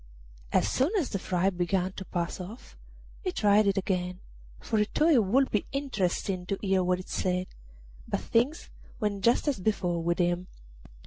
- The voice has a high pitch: Yes, high, 195 Hz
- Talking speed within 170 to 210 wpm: Yes, average, 180 wpm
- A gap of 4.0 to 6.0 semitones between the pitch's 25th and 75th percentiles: No, average, 3.6 semitones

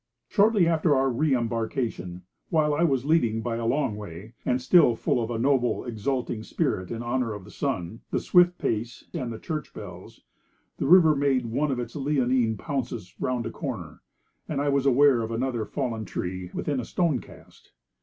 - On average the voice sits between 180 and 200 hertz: No, low, 125 Hz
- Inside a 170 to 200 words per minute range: Yes, average, 185 wpm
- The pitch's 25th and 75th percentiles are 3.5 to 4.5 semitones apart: Yes, average, 4.1 semitones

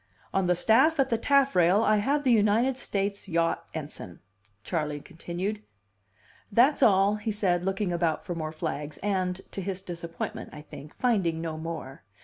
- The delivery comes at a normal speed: Yes, average, 160 wpm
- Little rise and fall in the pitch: No, average, 4.2 semitones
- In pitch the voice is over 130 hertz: Yes, high, 190 Hz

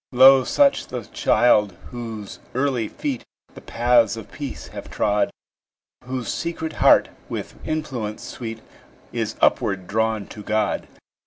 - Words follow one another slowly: Yes, slow, 130 wpm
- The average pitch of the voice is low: Yes, low, 120 Hz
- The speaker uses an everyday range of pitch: Yes, average, 3.6 semitones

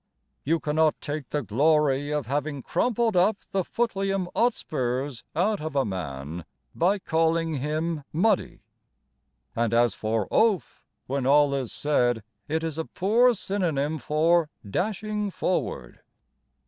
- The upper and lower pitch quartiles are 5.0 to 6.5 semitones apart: Yes, wide, 5.5 semitones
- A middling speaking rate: No, slow, 130 wpm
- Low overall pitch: No, medium, 155 Hz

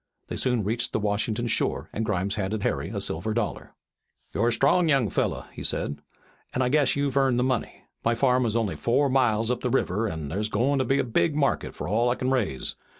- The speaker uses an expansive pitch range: No, average, 3.7 semitones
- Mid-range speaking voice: No, low, 120 Hz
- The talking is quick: Yes, fast, 225 wpm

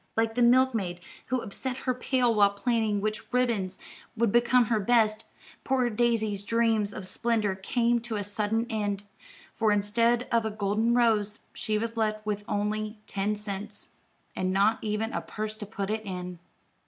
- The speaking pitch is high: Yes, high, 215 Hz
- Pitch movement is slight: Yes, narrow, 2.3 semitones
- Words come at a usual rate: Yes, average, 170 wpm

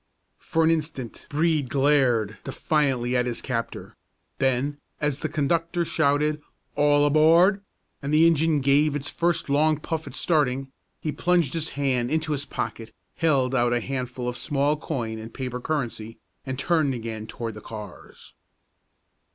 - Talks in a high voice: No, medium, 140 Hz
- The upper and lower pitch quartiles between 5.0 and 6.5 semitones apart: No, average, 3.8 semitones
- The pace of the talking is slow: No, average, 150 wpm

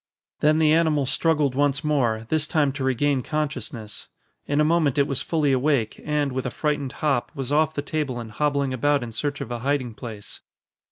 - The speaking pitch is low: No, medium, 145 Hz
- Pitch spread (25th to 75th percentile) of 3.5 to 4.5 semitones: No, average, 2.8 semitones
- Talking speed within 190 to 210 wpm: Yes, average, 200 wpm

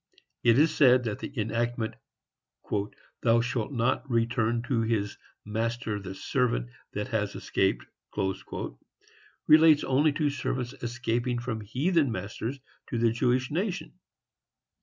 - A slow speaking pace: Yes, slow, 125 wpm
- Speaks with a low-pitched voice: Yes, low, 120 Hz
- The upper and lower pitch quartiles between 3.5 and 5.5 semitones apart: No, average, 2.8 semitones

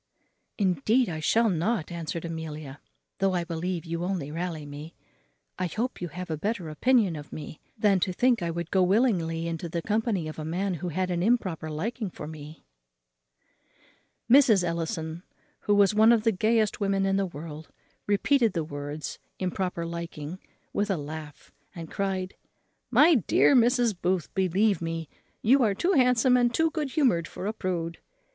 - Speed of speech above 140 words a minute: Yes, average, 170 wpm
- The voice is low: No, medium, 180 Hz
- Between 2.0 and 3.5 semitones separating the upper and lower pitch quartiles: No, average, 4.9 semitones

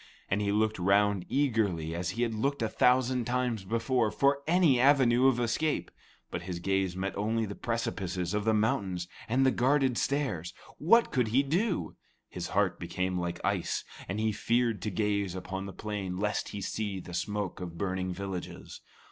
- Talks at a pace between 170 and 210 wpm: Yes, average, 180 wpm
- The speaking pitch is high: No, low, 105 Hz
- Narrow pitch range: No, average, 4.8 semitones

